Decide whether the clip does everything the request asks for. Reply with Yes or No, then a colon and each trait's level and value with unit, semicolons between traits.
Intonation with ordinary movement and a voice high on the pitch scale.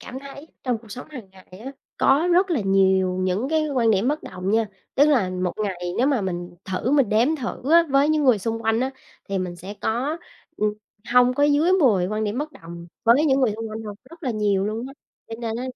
No: wide, 6.1 semitones; high, 230 Hz